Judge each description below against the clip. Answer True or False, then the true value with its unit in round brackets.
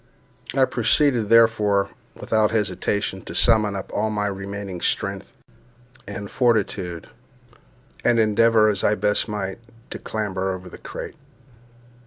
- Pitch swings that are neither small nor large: False (2.2 semitones)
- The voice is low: True (105 Hz)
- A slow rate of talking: True (125 wpm)